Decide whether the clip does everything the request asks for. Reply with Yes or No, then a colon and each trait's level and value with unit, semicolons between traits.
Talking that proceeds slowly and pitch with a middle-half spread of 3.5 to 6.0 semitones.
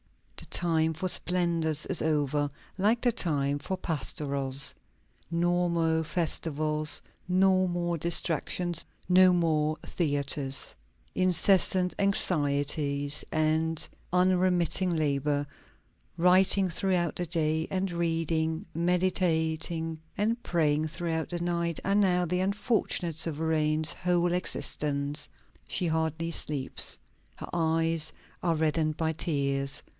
No: slow, 105 wpm; average, 2.7 semitones